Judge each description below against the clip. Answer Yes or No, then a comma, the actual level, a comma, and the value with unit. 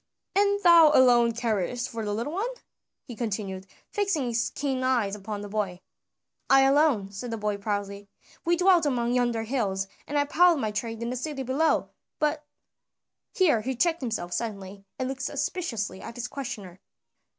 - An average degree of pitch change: No, wide, 5.7 semitones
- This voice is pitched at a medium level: No, high, 240 Hz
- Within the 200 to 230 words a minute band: No, average, 175 wpm